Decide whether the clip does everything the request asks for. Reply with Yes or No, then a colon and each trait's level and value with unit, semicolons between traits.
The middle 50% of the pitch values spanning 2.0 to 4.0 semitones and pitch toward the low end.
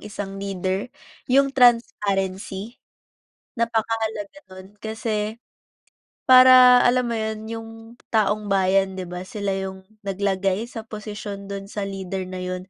No: average, 2.7 semitones; high, 205 Hz